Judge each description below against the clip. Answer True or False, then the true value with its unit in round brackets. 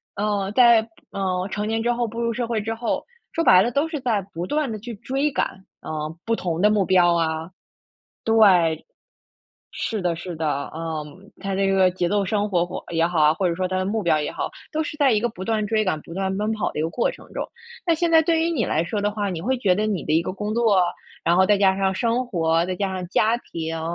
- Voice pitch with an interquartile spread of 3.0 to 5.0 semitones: True (4.4 semitones)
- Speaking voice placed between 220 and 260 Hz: False (195 Hz)